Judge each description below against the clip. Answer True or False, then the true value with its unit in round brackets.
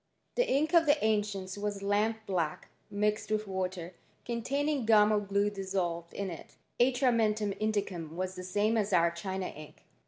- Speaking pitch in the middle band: False (205 Hz)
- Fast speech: False (165 wpm)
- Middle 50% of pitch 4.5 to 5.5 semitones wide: False (2.8 semitones)